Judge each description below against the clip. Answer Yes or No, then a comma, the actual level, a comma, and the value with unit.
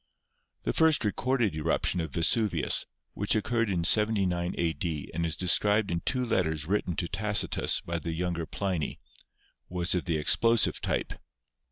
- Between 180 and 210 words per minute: No, average, 150 wpm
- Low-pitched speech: Yes, very low, 90 Hz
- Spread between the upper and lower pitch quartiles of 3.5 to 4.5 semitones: Yes, average, 4.2 semitones